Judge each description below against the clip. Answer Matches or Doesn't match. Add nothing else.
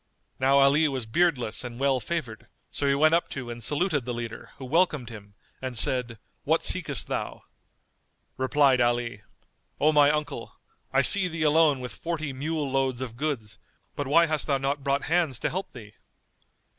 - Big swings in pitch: Doesn't match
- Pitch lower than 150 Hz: Matches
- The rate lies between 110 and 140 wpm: Doesn't match